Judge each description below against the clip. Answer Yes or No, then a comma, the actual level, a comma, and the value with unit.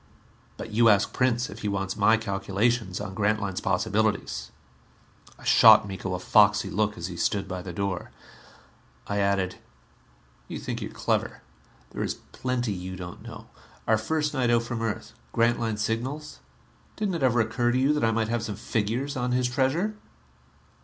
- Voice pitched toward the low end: Yes, low, 110 Hz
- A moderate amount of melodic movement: Yes, average, 3.5 semitones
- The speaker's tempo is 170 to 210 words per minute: Yes, average, 175 wpm